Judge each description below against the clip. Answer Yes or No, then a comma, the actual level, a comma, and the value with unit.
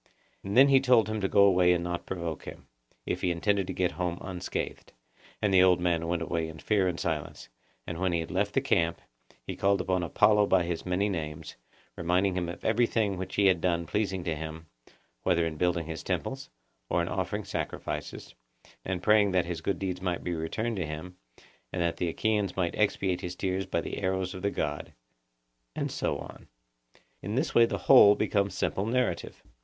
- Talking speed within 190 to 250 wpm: Yes, average, 200 wpm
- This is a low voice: Yes, very low, 90 Hz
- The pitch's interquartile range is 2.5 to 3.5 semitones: Yes, average, 3.0 semitones